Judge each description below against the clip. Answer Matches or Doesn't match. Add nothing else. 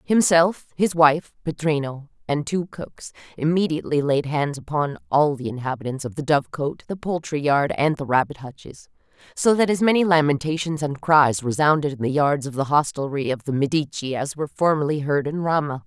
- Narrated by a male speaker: Doesn't match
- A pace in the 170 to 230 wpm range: Matches